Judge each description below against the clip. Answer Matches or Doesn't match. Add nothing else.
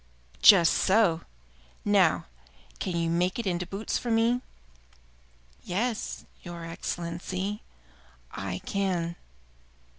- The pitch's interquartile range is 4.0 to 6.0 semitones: Doesn't match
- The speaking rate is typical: Doesn't match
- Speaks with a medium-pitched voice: Matches